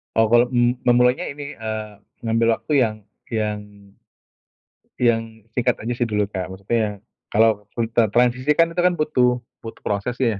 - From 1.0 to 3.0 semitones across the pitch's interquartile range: Yes, narrow, 2.4 semitones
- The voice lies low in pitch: Yes, low, 115 Hz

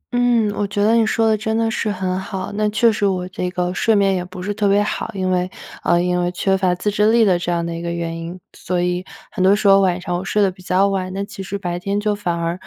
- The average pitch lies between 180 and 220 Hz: Yes, high, 190 Hz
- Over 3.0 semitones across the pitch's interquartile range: No, narrow, 2.5 semitones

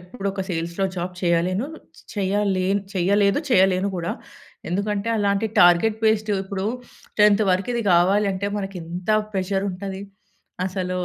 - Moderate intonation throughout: No, narrow, 1.8 semitones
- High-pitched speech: Yes, high, 195 Hz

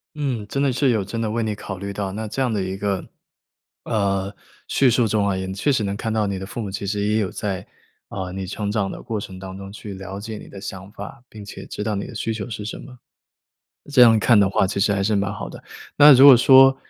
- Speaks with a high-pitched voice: No, low, 105 Hz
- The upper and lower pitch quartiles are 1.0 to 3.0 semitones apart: Yes, narrow, 2.6 semitones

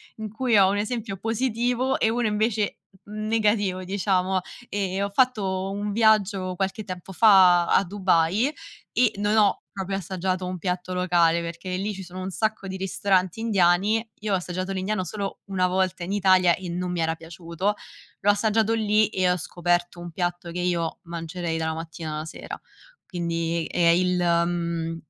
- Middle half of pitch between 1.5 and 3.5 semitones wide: Yes, average, 2.9 semitones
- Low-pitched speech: No, medium, 185 Hz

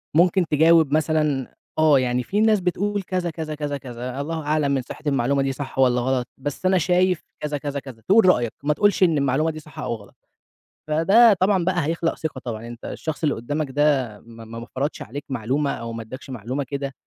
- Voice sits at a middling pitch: Yes, medium, 145 Hz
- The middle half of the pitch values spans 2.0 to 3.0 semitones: No, average, 4.2 semitones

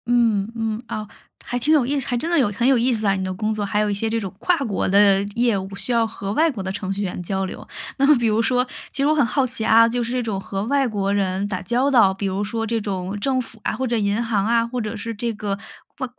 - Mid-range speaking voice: No, high, 225 Hz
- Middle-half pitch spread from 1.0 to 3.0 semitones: No, average, 3.4 semitones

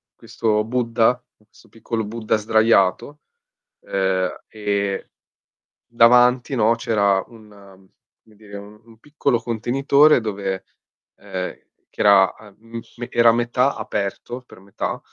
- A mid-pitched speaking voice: No, low, 110 Hz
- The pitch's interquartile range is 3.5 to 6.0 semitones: No, average, 2.8 semitones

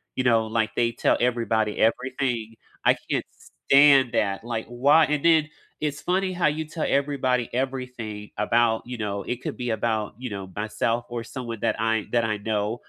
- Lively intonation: No, average, 3.2 semitones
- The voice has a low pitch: Yes, low, 120 Hz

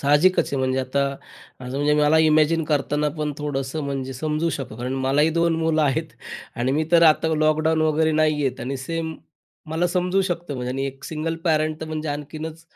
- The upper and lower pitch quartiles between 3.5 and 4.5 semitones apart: No, average, 2.7 semitones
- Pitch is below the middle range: No, medium, 150 Hz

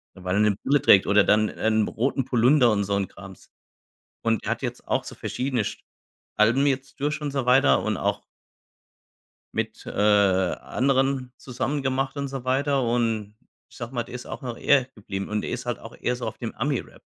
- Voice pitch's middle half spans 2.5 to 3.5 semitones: No, average, 4.0 semitones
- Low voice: Yes, low, 120 Hz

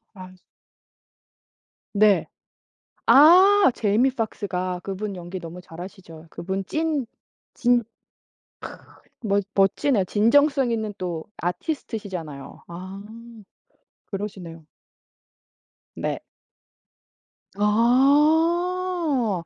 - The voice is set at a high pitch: Yes, high, 210 Hz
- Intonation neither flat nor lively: No, wide, 6.9 semitones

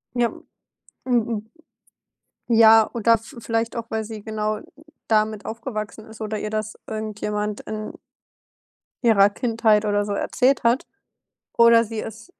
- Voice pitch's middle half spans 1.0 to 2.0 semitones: Yes, narrow, 1.4 semitones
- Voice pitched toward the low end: No, high, 220 Hz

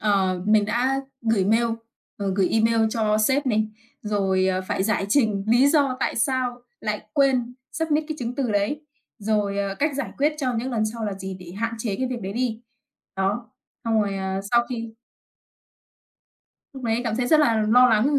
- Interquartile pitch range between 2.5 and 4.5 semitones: Yes, average, 3.7 semitones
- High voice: Yes, high, 225 Hz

